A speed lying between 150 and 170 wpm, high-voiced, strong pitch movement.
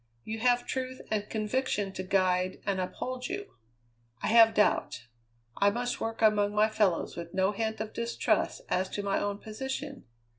No: average, 165 wpm; high, 215 Hz; average, 3.5 semitones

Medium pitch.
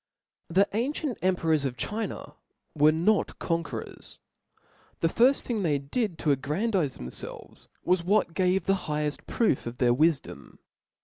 Yes: medium, 170 Hz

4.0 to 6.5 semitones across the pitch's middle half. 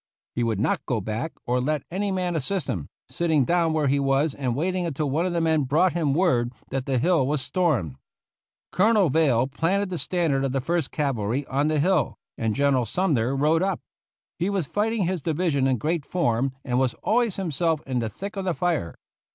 Yes: average, 5.1 semitones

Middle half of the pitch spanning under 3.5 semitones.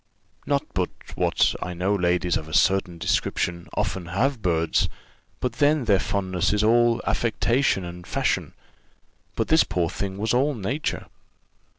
No: average, 5.0 semitones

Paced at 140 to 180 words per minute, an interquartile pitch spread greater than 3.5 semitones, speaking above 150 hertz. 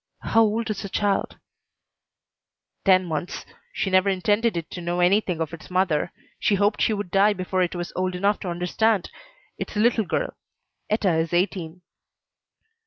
No: average, 170 wpm; average, 2.8 semitones; medium, 185 Hz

